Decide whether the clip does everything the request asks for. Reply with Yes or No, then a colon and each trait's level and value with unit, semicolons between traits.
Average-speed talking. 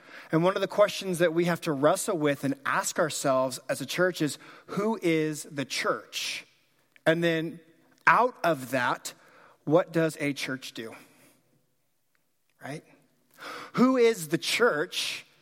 Yes: average, 145 wpm